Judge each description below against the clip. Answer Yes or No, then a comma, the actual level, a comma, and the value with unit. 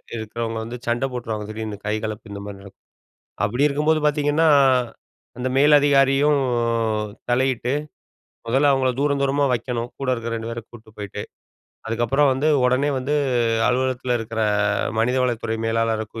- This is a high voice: No, low, 125 Hz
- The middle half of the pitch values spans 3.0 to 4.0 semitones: Yes, average, 3.4 semitones